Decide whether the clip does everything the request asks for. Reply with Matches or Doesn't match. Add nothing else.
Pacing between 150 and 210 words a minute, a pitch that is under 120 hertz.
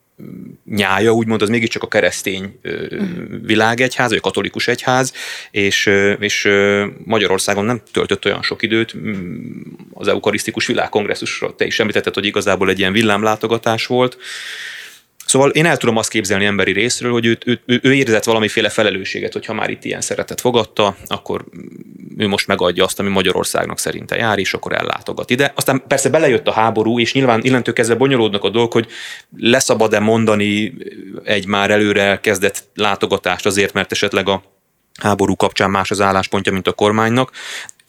Matches